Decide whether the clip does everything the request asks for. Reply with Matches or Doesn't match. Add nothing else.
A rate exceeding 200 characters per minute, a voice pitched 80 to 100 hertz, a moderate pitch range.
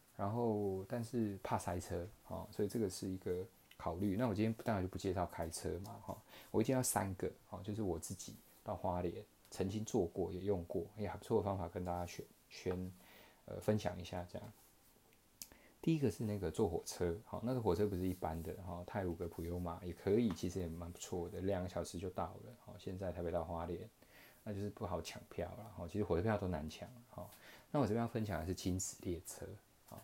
Matches